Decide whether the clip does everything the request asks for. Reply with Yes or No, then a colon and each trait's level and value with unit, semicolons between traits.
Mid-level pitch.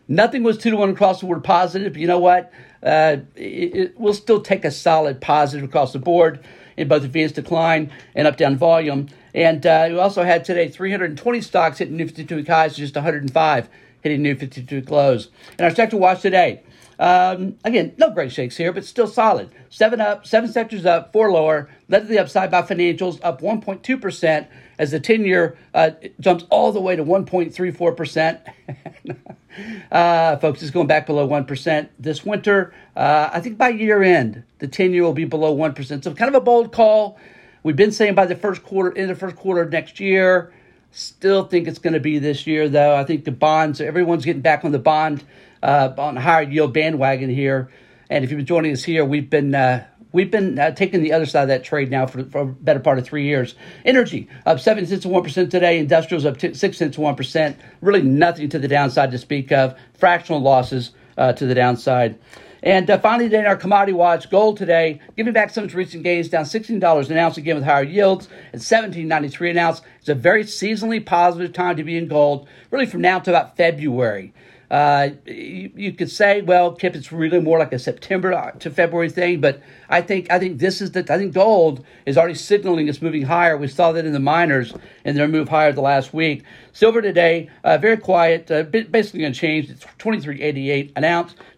Yes: medium, 165 Hz